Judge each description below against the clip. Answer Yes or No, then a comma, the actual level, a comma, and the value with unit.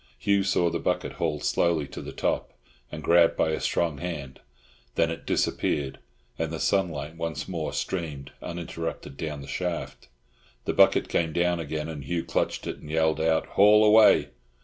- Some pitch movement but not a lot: No, narrow, 2.3 semitones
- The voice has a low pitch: Yes, very low, 80 Hz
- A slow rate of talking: No, average, 170 wpm